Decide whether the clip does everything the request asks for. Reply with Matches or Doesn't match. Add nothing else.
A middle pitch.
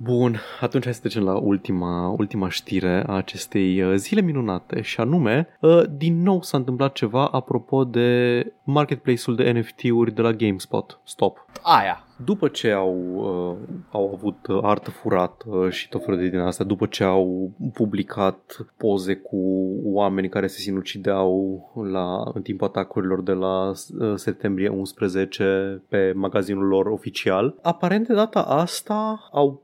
Doesn't match